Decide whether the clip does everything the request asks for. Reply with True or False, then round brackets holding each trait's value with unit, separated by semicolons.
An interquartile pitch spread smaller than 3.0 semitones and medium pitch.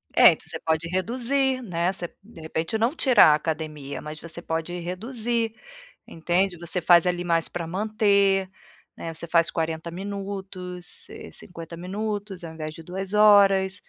False (3.5 semitones; 180 Hz)